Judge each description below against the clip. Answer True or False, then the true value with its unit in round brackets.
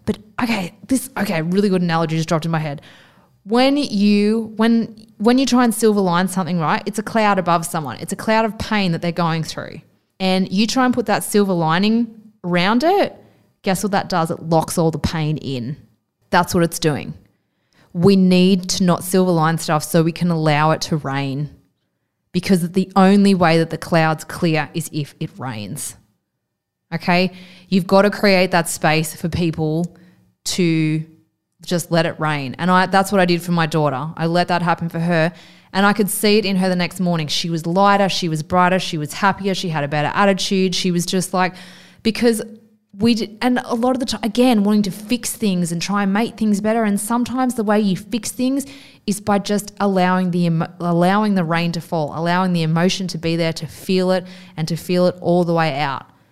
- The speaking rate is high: True (210 wpm)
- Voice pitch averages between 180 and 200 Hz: True (185 Hz)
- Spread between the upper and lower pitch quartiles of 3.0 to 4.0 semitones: True (3.7 semitones)